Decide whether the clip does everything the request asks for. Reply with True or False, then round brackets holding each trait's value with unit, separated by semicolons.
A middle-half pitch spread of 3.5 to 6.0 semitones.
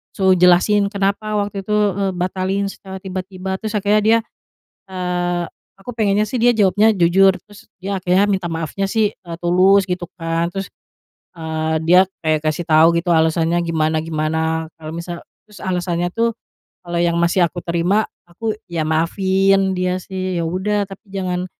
False (2.6 semitones)